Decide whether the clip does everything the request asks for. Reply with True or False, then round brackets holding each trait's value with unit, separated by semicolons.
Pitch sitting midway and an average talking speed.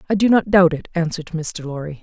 False (170 Hz; 235 wpm)